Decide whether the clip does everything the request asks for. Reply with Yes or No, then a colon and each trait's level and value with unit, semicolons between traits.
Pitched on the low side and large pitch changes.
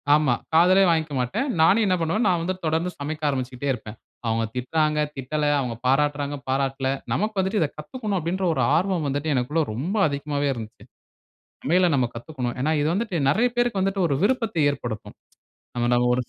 No: medium, 150 Hz; wide, 5.7 semitones